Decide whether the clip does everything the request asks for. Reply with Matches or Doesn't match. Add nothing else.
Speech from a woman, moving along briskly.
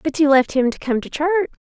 Matches